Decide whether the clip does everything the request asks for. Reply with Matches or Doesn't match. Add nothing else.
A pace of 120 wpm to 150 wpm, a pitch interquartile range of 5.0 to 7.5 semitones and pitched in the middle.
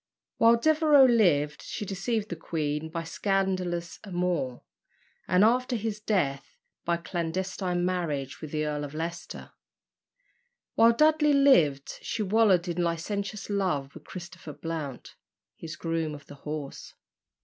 Matches